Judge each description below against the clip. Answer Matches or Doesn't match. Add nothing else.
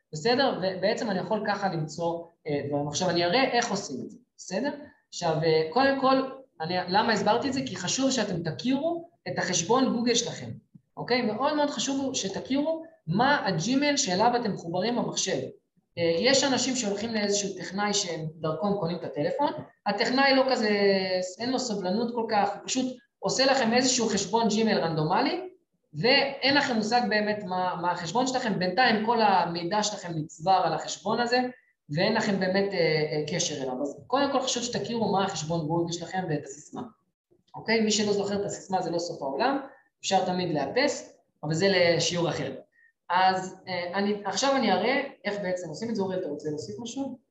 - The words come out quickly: Matches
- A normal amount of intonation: Doesn't match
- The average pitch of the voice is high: Matches